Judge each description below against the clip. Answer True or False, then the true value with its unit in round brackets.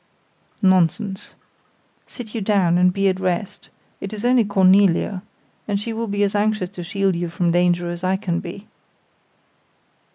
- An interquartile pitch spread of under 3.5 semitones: True (2.6 semitones)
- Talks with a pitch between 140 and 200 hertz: True (190 Hz)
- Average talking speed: True (160 wpm)